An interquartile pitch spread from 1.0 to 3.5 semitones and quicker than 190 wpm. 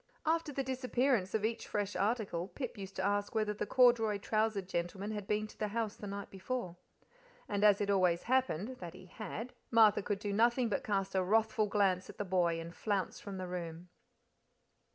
Yes: average, 2.9 semitones; average, 200 wpm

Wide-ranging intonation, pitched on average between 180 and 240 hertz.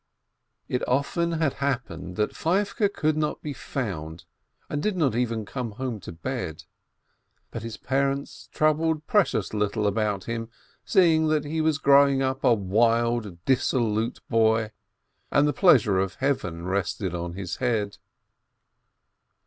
No: wide, 5.8 semitones; low, 120 Hz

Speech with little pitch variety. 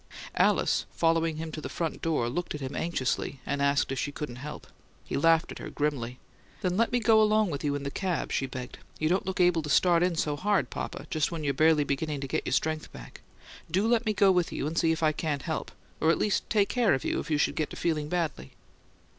No: average, 3.7 semitones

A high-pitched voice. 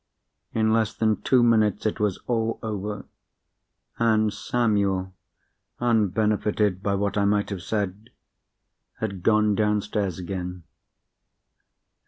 No: low, 105 Hz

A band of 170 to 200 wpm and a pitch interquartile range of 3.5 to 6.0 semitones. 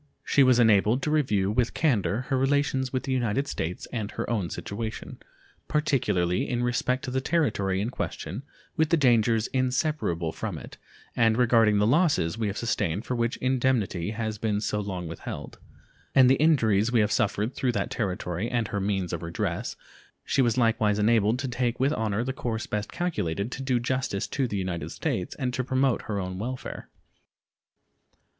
Yes: average, 180 wpm; average, 4.1 semitones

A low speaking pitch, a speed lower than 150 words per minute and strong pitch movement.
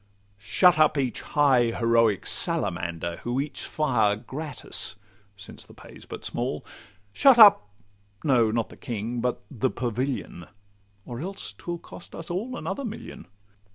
Yes: low, 125 Hz; average, 140 wpm; wide, 6.3 semitones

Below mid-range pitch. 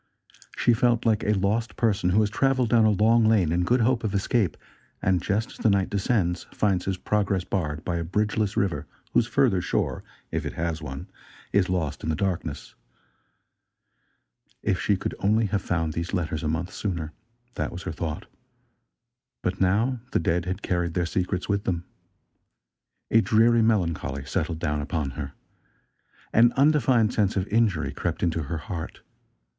Yes: very low, 95 Hz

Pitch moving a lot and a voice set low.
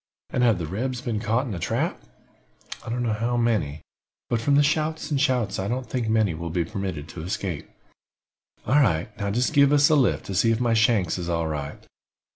Yes: wide, 5.8 semitones; low, 110 Hz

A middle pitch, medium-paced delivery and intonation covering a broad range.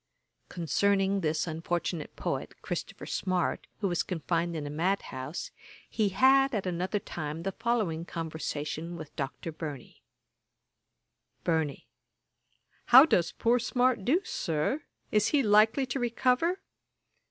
No: medium, 180 Hz; slow, 125 wpm; wide, 6.5 semitones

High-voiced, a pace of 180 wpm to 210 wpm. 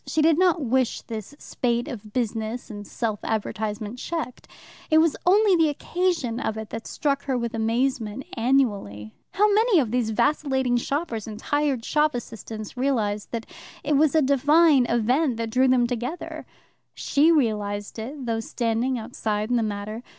No: high, 245 Hz; average, 165 wpm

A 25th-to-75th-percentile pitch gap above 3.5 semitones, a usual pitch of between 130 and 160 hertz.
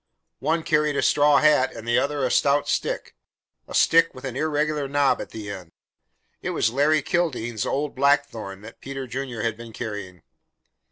Yes: average, 4.4 semitones; low, 135 Hz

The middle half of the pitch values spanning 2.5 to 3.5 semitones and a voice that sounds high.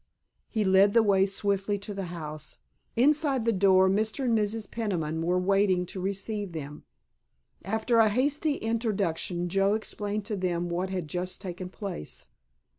Yes: average, 3.2 semitones; high, 195 Hz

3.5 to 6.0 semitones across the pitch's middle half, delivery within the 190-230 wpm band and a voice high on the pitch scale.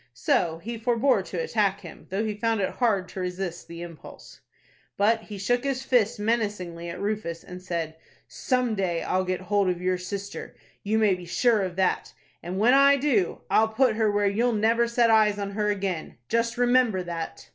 Yes: average, 4.0 semitones; average, 195 wpm; high, 205 Hz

